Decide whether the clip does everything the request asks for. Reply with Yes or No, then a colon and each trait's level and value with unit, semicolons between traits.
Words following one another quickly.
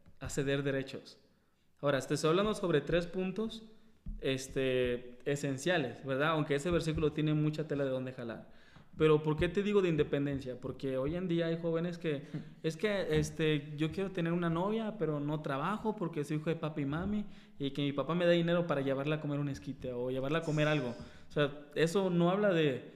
Yes: fast, 200 wpm